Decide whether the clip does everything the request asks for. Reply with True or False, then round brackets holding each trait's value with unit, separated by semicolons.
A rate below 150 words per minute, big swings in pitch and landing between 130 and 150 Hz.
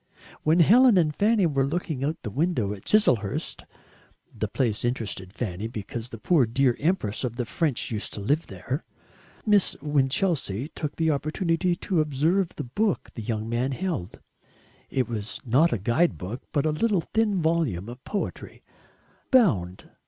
False (165 wpm; 6.9 semitones; 140 Hz)